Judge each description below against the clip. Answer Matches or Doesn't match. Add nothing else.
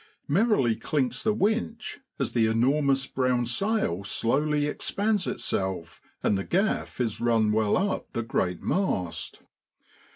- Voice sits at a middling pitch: Doesn't match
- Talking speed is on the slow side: Matches